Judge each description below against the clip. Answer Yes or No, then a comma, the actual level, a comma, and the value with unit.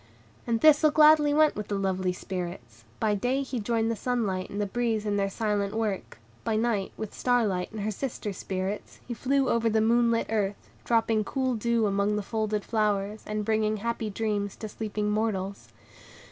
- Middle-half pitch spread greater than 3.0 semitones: No, narrow, 2.6 semitones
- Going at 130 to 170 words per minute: No, average, 190 wpm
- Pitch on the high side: Yes, high, 215 Hz